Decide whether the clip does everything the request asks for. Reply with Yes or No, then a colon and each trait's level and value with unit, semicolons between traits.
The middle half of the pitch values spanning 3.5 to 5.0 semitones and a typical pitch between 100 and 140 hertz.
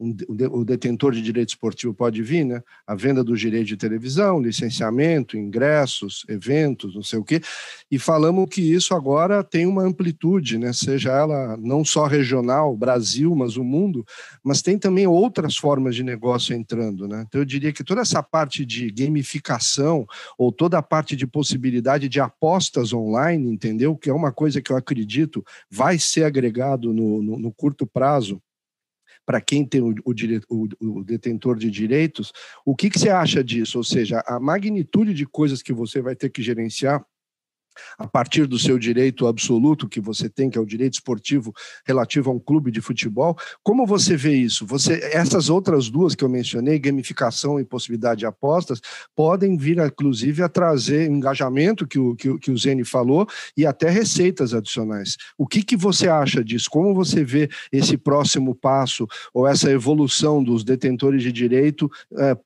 Yes: average, 4.3 semitones; low, 135 Hz